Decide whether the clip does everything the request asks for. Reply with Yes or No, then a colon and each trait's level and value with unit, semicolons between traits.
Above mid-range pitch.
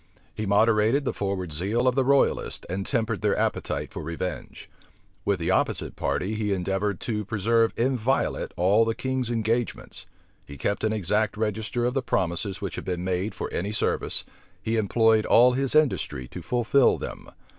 No: low, 110 Hz